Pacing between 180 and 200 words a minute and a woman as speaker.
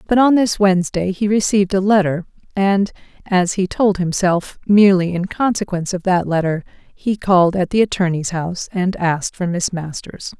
No: average, 160 wpm; female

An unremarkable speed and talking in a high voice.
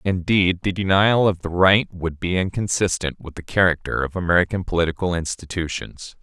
No: average, 155 wpm; very low, 90 Hz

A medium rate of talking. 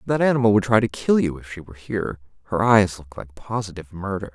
No: fast, 235 wpm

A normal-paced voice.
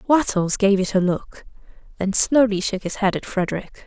Yes: average, 185 wpm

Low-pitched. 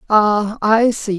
No: high, 215 Hz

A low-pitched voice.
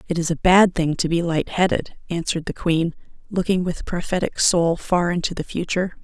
No: medium, 175 Hz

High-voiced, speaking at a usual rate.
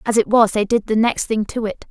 No: high, 220 Hz; fast, 315 wpm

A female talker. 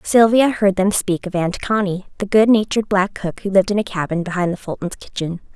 Yes: female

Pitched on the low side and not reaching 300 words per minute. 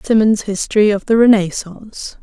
No: high, 210 Hz; slow, 135 wpm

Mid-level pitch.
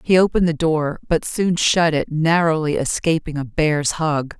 Yes: medium, 160 Hz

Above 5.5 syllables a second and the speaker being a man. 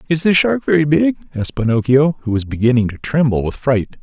Yes: 5.9 syllables/s; male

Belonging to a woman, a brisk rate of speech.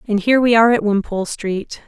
Yes: female; fast, 225 wpm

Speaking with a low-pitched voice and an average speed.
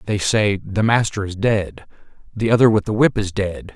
No: low, 105 Hz; fast, 210 wpm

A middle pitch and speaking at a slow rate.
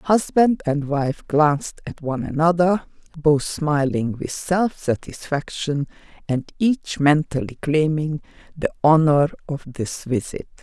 Yes: medium, 155 Hz; slow, 120 wpm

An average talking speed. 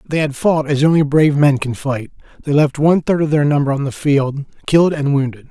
No: fast, 240 wpm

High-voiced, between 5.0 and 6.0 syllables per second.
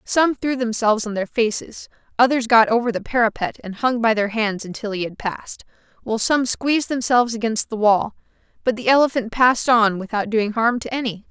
Yes: high, 230 Hz; 5.6 syllables/s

